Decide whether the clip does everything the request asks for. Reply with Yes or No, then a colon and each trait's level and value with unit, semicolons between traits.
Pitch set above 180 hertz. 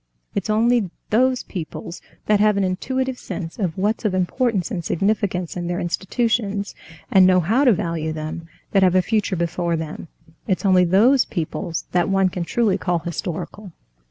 Yes: high, 190 Hz